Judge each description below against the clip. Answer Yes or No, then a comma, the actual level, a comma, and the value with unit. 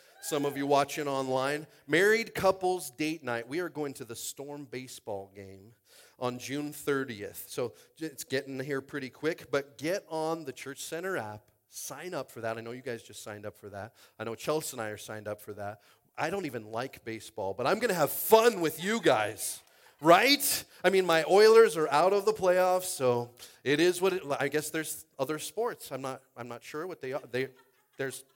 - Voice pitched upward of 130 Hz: Yes, medium, 140 Hz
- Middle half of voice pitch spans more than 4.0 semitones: Yes, wide, 5.5 semitones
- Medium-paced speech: No, fast, 210 wpm